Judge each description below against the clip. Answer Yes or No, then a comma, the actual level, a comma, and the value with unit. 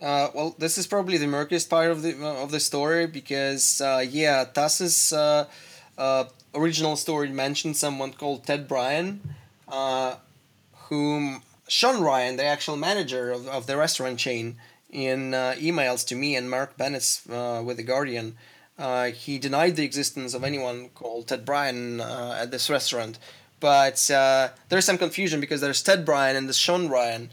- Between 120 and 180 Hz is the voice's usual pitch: Yes, low, 135 Hz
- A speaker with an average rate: Yes, average, 170 wpm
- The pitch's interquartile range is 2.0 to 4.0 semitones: Yes, average, 2.9 semitones